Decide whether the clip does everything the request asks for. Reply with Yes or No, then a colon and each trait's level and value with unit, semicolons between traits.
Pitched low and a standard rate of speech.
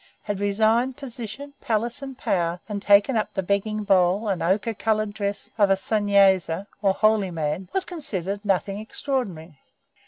No: high, 205 Hz; average, 155 wpm